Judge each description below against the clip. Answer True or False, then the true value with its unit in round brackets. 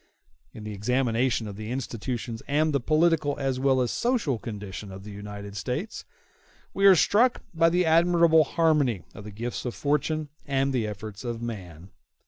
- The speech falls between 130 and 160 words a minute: False (170 wpm)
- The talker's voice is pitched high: False (125 Hz)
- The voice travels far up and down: True (6.5 semitones)